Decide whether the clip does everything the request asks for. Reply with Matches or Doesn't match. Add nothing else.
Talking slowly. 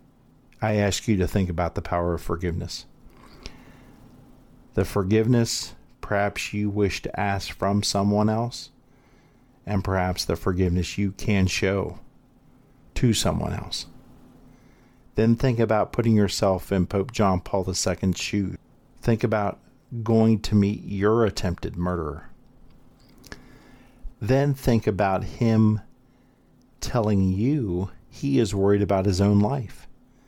Matches